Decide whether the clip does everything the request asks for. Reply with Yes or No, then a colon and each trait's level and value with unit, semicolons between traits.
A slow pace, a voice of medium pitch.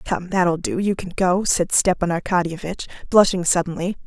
No: average, 160 wpm; medium, 180 Hz